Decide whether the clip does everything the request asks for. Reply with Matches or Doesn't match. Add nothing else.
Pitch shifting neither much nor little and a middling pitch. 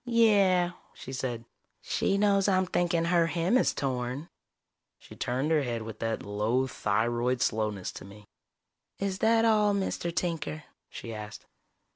Doesn't match